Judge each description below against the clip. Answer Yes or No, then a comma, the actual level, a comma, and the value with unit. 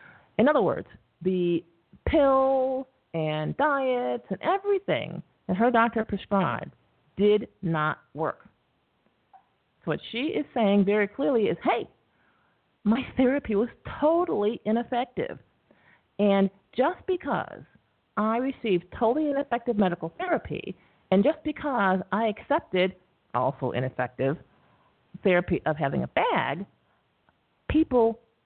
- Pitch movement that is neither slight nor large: No, wide, 6.3 semitones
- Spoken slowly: Yes, slow, 110 wpm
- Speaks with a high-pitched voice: Yes, high, 210 Hz